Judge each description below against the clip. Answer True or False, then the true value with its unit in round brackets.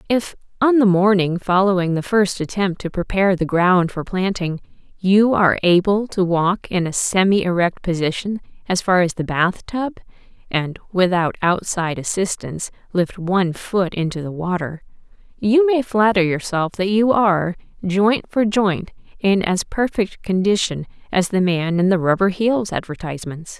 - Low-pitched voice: False (185 Hz)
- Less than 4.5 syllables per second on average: True (4.1 syllables/s)